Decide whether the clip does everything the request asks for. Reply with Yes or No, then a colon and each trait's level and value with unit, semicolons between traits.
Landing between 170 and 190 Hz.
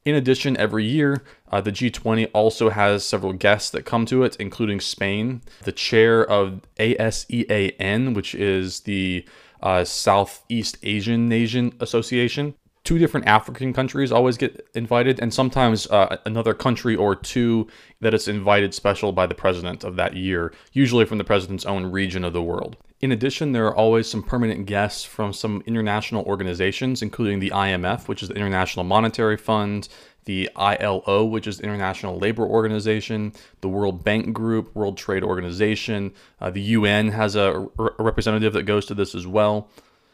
No: low, 105 Hz